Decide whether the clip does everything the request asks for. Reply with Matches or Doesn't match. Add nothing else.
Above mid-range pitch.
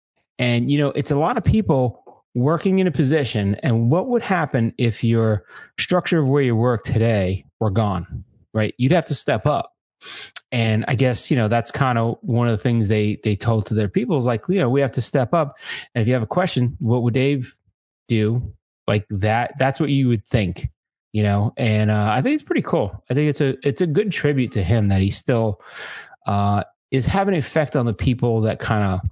Doesn't match